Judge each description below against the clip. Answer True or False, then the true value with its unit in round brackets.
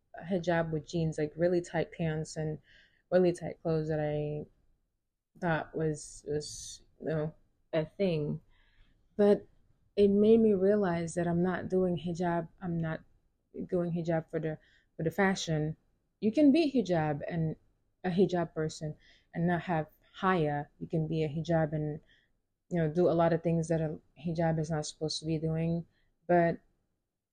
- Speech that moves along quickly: False (160 wpm)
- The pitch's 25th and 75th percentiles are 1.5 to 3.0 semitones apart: True (2.4 semitones)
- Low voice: False (160 Hz)